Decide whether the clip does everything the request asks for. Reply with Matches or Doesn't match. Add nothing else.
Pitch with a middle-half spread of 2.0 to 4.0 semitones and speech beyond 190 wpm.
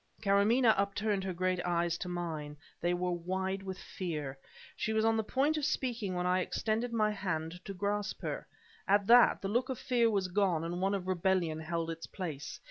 Matches